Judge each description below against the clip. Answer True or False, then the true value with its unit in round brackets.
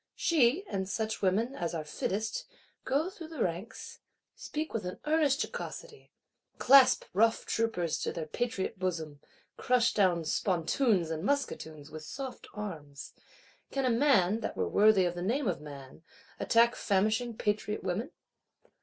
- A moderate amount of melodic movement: False (6.3 semitones)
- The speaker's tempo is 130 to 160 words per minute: True (145 wpm)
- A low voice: False (210 Hz)